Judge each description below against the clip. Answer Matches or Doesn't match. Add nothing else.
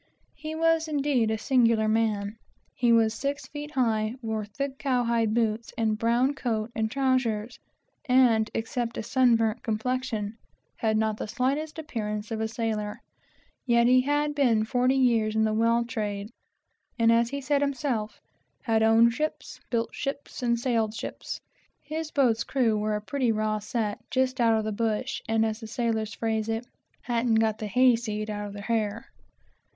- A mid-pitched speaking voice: Doesn't match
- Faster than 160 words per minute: Matches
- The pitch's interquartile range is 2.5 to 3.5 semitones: Matches